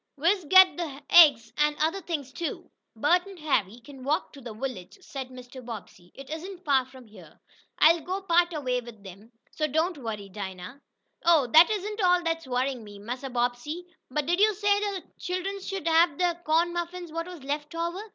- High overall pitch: Yes, very high, 305 Hz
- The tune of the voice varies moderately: No, wide, 5.9 semitones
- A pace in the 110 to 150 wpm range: No, average, 195 wpm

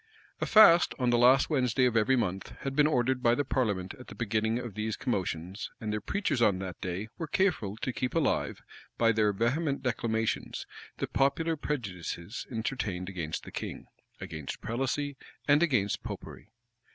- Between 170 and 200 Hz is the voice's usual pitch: No, low, 120 Hz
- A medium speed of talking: Yes, average, 175 wpm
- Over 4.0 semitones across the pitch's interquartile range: Yes, average, 4.9 semitones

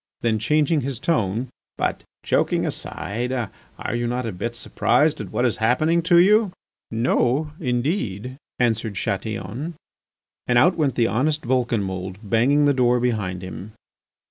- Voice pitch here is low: Yes, low, 120 Hz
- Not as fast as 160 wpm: Yes, average, 145 wpm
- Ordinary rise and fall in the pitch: Yes, average, 4.7 semitones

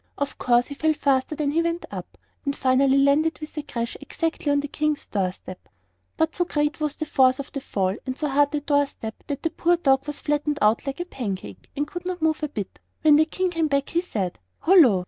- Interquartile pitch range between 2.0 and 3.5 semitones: Yes, average, 3.0 semitones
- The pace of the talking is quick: Yes, fast, 240 wpm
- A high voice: Yes, very high, 290 Hz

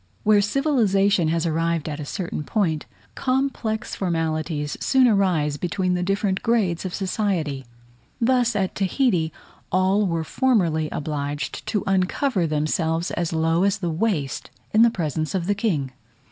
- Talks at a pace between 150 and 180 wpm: No, average, 140 wpm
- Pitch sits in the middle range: Yes, medium, 180 Hz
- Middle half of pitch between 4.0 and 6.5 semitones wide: Yes, average, 4.6 semitones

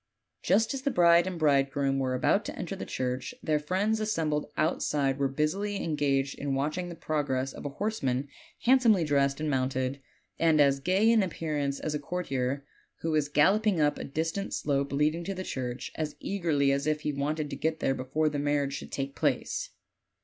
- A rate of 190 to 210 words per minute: Yes, average, 200 wpm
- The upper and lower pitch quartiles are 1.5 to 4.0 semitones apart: Yes, average, 3.7 semitones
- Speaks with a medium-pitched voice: Yes, medium, 150 Hz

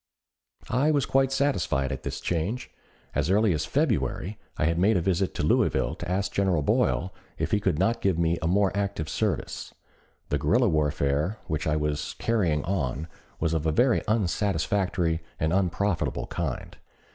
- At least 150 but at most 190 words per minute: Yes, average, 170 wpm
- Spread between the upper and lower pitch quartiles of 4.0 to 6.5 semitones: Yes, average, 4.7 semitones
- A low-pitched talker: Yes, very low, 90 Hz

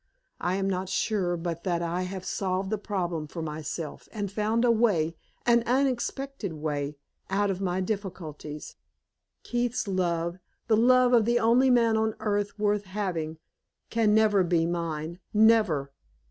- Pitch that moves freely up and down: No, average, 4.5 semitones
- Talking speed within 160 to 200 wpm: No, average, 150 wpm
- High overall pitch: Yes, high, 195 Hz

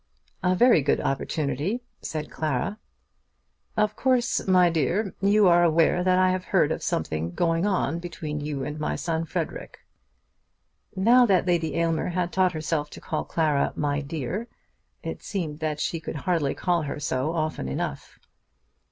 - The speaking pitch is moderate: Yes, medium, 165 Hz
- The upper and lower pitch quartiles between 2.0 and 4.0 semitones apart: Yes, average, 3.6 semitones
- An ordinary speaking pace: Yes, average, 160 wpm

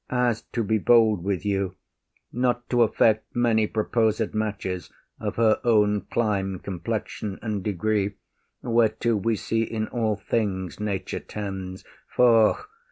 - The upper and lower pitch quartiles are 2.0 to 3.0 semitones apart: Yes, narrow, 2.6 semitones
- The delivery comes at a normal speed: No, slow, 130 wpm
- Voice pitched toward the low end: Yes, low, 110 Hz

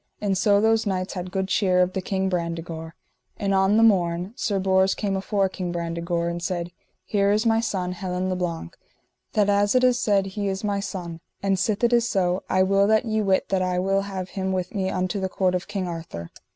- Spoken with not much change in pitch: Yes, narrow, 1.9 semitones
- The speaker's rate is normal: No, fast, 225 wpm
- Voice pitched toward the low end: No, high, 190 Hz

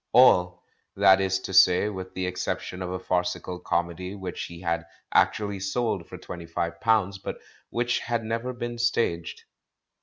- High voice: No, very low, 95 Hz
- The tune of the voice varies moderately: Yes, average, 3.7 semitones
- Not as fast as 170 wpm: Yes, average, 160 wpm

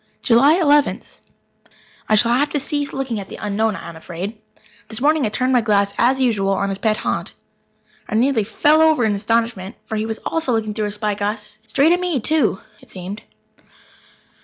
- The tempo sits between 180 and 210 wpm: Yes, average, 195 wpm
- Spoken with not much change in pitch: No, average, 4.7 semitones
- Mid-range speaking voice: No, high, 225 Hz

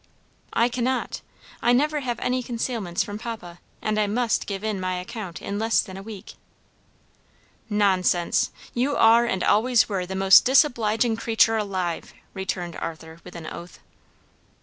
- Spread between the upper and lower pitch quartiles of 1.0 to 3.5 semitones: No, average, 4.2 semitones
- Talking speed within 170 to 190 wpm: No, average, 150 wpm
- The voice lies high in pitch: Yes, high, 210 Hz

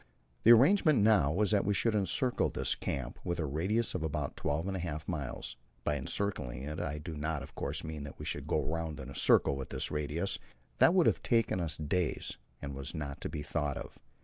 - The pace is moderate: No, fast, 220 wpm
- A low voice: Yes, very low, 80 Hz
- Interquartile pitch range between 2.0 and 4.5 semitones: No, average, 5.3 semitones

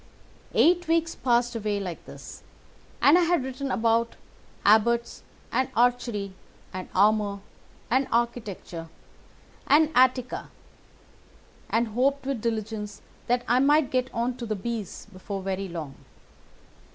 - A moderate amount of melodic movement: Yes, average, 3.8 semitones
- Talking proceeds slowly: Yes, slow, 125 wpm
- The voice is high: Yes, high, 235 Hz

